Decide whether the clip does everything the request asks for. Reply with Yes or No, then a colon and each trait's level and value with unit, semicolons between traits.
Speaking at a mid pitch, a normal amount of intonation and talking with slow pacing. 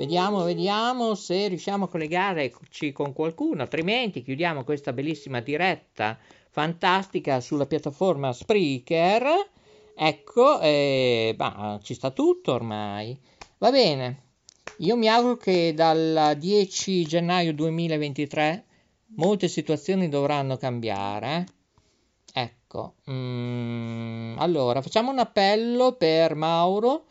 No: medium, 160 Hz; wide, 5.7 semitones; slow, 100 wpm